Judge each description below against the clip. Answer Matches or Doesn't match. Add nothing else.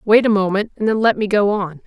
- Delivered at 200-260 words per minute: Doesn't match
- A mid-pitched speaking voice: Doesn't match